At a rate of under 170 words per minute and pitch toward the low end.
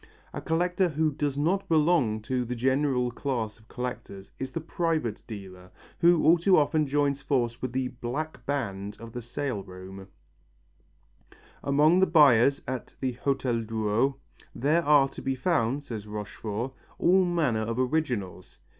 Yes: average, 155 wpm; low, 130 Hz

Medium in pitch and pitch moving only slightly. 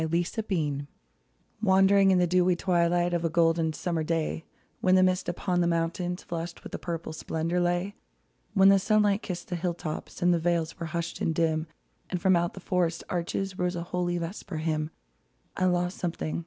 Yes: medium, 175 Hz; narrow, 1.6 semitones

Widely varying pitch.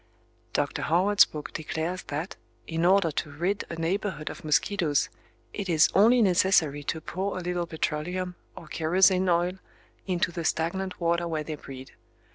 No: average, 2.9 semitones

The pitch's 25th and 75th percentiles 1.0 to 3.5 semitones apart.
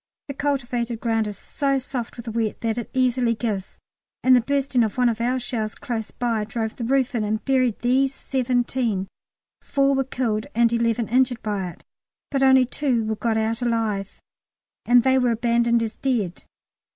Yes: narrow, 2.5 semitones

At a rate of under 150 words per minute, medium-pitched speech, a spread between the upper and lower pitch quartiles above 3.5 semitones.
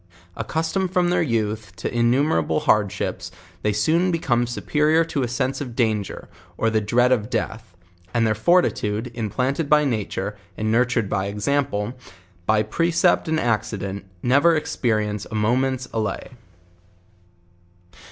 No: average, 140 wpm; low, 120 Hz; average, 5.2 semitones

